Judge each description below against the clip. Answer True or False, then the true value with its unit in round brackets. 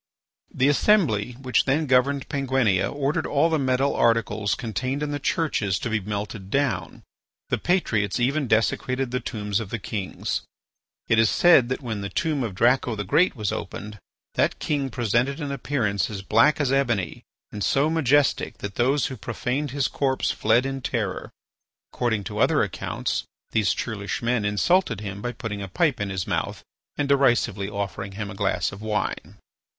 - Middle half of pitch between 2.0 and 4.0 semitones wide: False (5.1 semitones)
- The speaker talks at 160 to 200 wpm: True (175 wpm)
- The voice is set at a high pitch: False (120 Hz)